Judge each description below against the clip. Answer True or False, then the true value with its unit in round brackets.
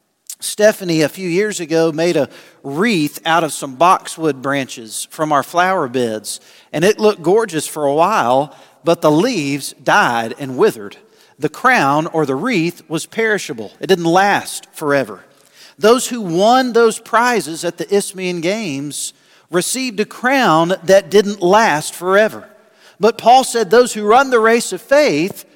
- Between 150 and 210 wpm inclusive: True (155 wpm)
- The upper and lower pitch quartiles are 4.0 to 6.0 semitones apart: True (5.6 semitones)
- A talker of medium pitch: True (180 Hz)